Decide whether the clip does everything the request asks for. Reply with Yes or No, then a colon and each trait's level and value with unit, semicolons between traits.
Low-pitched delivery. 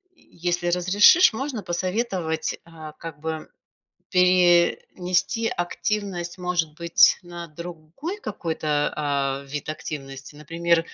No: medium, 170 Hz